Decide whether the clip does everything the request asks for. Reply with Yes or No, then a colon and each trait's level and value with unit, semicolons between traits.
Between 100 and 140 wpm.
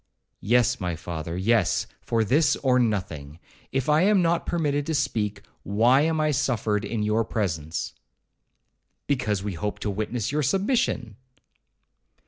Yes: slow, 135 wpm